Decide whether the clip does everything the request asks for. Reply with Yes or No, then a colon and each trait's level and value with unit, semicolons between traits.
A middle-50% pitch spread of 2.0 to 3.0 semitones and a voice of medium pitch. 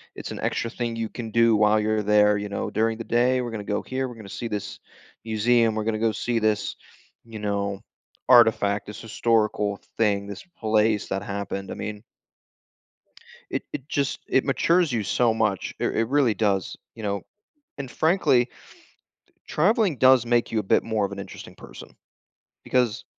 No: narrow, 2.6 semitones; low, 110 Hz